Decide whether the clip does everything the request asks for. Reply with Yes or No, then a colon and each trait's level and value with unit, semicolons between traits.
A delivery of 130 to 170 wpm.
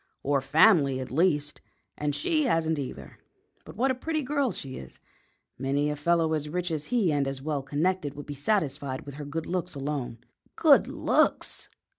No: average, 180 wpm